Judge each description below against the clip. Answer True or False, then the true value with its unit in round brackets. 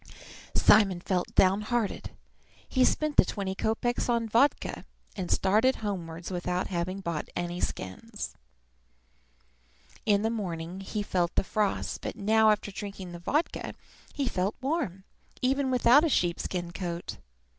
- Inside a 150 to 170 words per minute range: False (140 wpm)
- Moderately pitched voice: False (200 Hz)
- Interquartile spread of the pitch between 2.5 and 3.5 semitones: False (4.3 semitones)